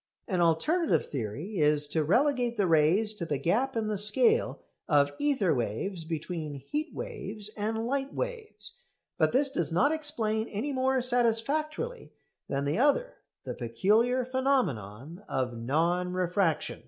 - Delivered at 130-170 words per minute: Yes, average, 140 wpm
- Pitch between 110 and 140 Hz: No, high, 210 Hz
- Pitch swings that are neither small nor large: No, wide, 8.9 semitones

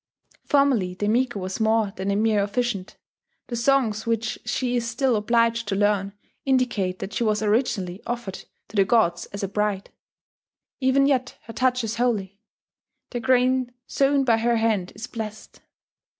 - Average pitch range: Yes, average, 3.4 semitones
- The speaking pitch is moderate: No, high, 225 Hz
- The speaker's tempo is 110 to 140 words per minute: No, average, 165 wpm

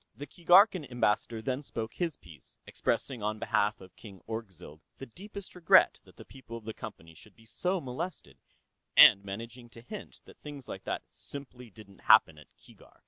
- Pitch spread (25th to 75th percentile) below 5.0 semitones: No, wide, 5.4 semitones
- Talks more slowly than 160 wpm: No, average, 180 wpm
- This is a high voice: No, low, 115 Hz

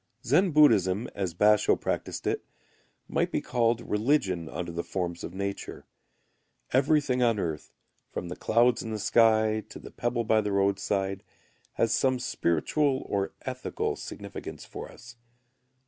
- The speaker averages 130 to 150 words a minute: Yes, average, 145 wpm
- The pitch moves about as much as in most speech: Yes, average, 4.2 semitones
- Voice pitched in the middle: No, low, 110 Hz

